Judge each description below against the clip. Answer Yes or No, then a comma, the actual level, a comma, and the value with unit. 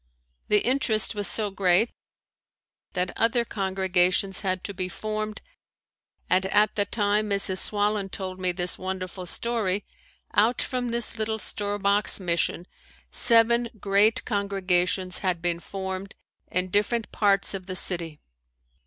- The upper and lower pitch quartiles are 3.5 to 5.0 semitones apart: No, narrow, 2.5 semitones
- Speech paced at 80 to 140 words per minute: Yes, slow, 135 wpm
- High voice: Yes, high, 200 Hz